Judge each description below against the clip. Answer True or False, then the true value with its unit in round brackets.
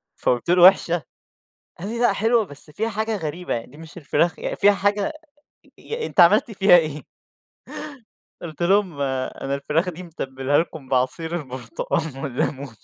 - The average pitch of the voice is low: False (165 Hz)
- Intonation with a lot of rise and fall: True (5.7 semitones)